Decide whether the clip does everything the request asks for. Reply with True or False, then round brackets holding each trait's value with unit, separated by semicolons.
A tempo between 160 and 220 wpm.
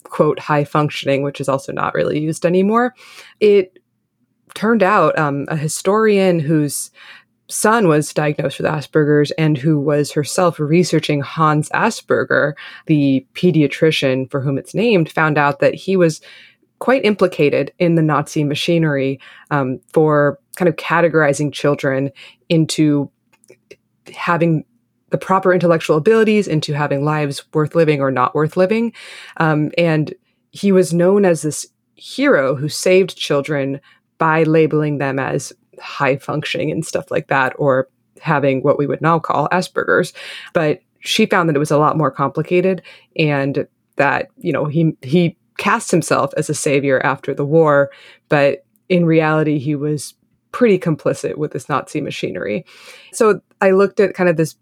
False (150 wpm)